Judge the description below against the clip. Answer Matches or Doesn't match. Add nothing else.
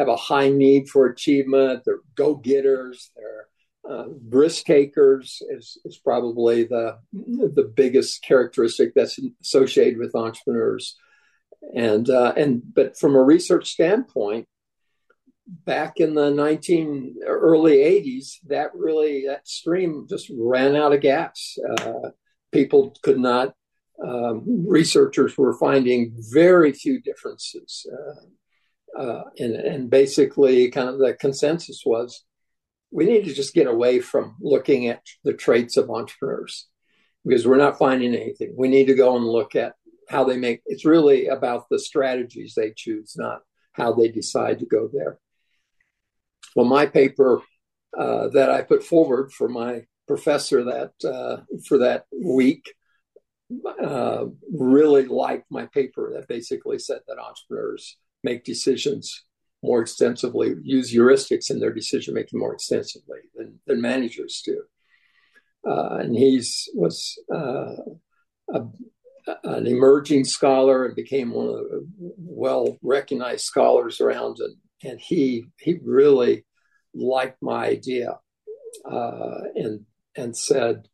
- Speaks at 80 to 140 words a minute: Matches